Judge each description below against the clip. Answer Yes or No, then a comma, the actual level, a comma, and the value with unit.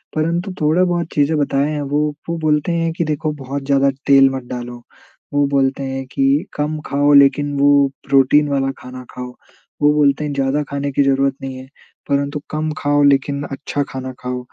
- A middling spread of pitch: No, narrow, 1.7 semitones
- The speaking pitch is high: No, medium, 140 Hz